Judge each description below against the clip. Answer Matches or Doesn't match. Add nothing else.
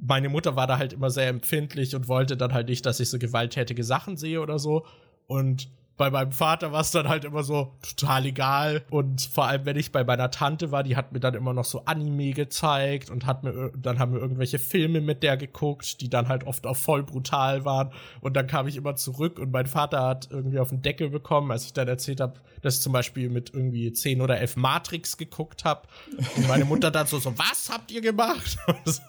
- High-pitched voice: Doesn't match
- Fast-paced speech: Matches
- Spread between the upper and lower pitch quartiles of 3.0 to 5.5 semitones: Doesn't match